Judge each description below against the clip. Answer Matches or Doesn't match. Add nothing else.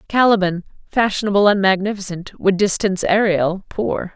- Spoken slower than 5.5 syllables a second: Matches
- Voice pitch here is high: Matches